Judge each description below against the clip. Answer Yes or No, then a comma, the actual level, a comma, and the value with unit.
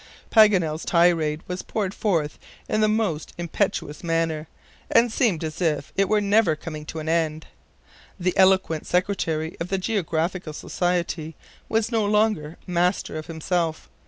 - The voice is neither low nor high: Yes, medium, 175 Hz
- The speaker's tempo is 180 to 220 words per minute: No, average, 150 wpm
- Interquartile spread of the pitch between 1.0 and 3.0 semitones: No, average, 4.1 semitones